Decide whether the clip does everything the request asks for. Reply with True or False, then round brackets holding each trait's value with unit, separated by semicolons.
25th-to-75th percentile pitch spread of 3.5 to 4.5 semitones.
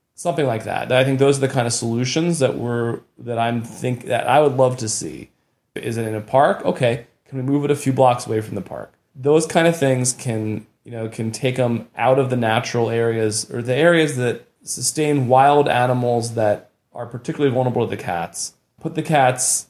False (2.8 semitones)